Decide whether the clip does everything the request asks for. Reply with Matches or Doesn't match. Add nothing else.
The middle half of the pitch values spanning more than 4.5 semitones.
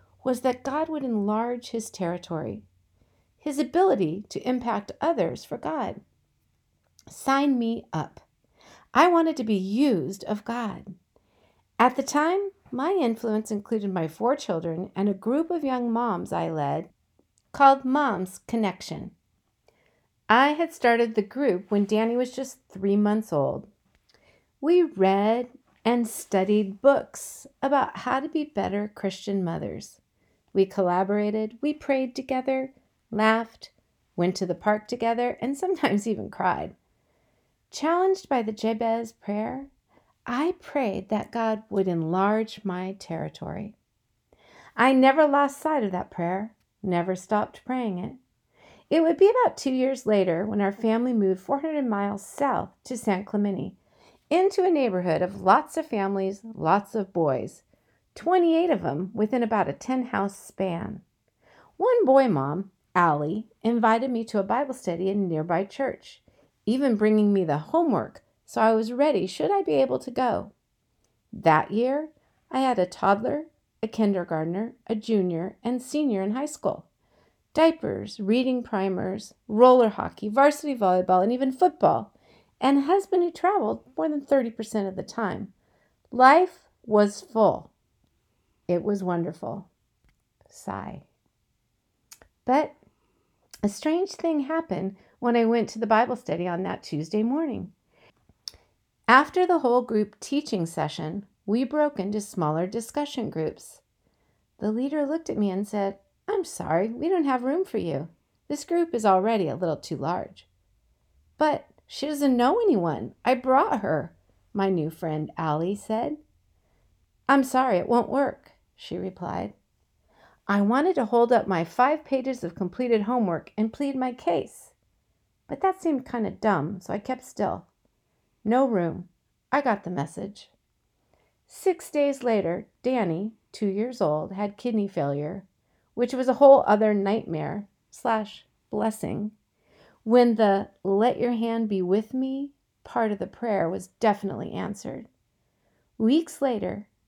Matches